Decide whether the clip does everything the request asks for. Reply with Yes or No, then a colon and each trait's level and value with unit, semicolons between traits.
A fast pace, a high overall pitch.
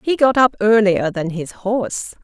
No: average, 190 wpm; high, 215 Hz